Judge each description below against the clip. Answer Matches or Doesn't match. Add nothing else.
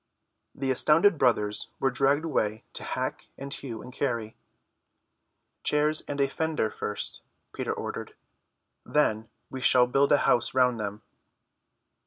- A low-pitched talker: Matches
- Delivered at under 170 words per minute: Matches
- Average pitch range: Matches